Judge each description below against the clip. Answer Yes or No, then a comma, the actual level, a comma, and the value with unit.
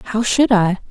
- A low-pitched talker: No, high, 220 Hz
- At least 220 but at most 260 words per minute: No, average, 200 wpm